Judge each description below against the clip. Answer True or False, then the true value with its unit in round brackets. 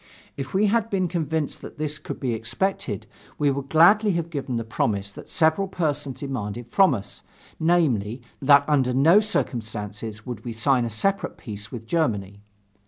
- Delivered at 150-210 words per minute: True (170 wpm)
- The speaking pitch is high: False (135 Hz)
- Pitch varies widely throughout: True (6.6 semitones)